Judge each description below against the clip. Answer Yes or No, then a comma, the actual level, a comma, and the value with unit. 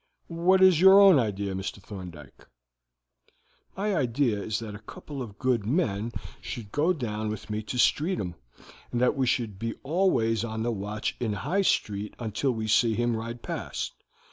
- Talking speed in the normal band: Yes, average, 170 wpm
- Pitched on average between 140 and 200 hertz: No, low, 115 Hz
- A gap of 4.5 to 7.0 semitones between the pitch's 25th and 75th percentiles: Yes, average, 5.2 semitones